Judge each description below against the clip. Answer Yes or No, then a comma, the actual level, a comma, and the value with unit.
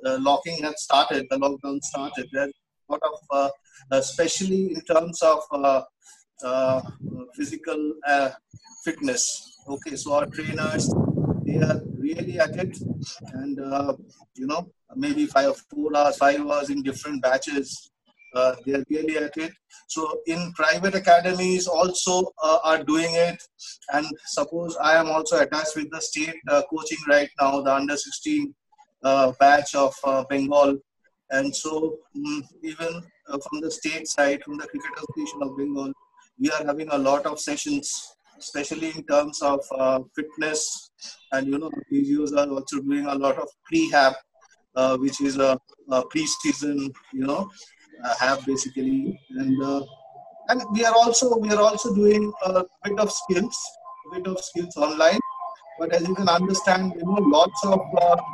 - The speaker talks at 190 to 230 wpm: No, average, 165 wpm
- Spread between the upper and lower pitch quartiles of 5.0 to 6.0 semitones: Yes, wide, 5.4 semitones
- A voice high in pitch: No, medium, 155 Hz